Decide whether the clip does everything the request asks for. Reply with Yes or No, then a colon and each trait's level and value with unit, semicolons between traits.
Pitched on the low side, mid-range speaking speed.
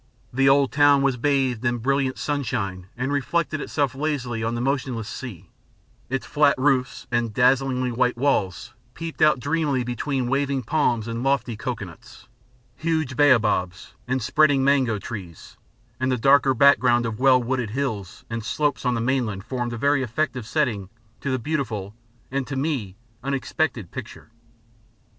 Yes: low, 130 Hz; average, 150 wpm